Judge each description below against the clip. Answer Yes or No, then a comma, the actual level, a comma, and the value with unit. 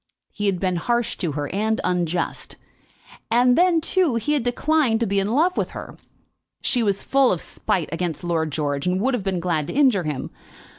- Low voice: No, high, 200 Hz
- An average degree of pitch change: No, wide, 6.3 semitones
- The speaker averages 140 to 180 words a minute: No, average, 200 wpm